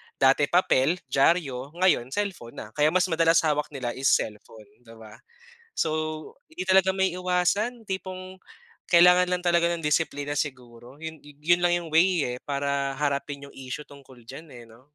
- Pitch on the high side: No, medium, 150 Hz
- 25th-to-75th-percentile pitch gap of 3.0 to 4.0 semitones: No, average, 4.9 semitones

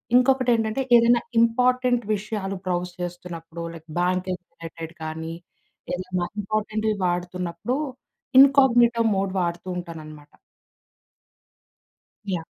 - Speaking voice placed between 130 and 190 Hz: Yes, medium, 185 Hz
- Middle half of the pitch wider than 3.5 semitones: Yes, average, 5.3 semitones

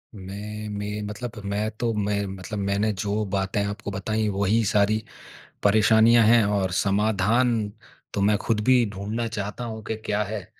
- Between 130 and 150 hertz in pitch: No, low, 105 Hz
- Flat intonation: Yes, narrow, 1.6 semitones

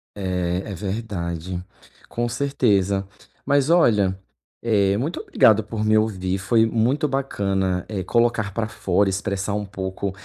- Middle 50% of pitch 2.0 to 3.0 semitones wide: No, average, 3.4 semitones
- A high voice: No, low, 100 Hz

